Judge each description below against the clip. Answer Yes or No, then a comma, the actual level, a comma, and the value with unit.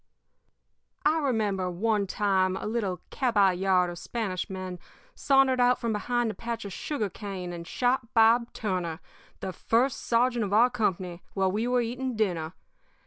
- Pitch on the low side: No, high, 215 Hz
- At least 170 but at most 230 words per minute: No, average, 155 wpm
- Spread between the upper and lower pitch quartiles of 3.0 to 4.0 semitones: No, average, 4.4 semitones